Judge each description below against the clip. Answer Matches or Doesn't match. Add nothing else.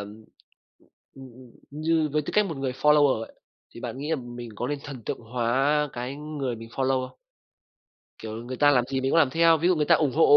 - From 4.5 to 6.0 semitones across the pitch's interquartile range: Doesn't match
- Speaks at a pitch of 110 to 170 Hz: Matches